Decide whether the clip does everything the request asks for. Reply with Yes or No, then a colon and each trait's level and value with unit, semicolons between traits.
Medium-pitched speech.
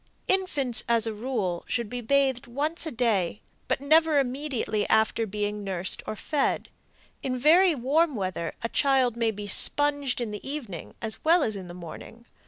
No: high, 240 Hz